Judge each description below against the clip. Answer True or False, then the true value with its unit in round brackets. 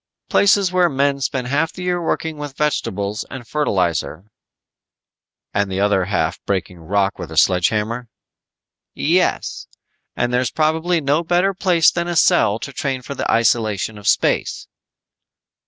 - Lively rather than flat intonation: True (8.0 semitones)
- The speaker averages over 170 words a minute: False (155 wpm)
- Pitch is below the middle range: True (130 Hz)